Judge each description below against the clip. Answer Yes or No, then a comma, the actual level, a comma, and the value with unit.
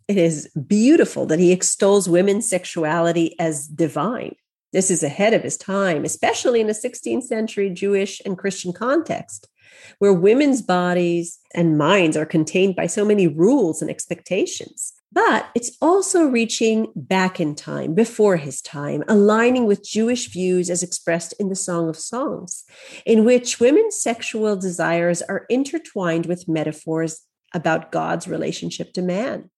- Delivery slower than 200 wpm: Yes, average, 150 wpm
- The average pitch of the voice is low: No, high, 190 Hz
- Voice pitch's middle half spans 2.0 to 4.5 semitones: No, average, 5.0 semitones